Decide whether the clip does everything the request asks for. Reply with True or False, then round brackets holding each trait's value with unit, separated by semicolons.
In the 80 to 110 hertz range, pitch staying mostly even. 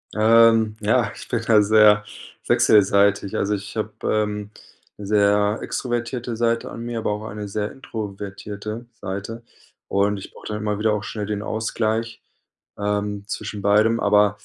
True (105 Hz; 1.5 semitones)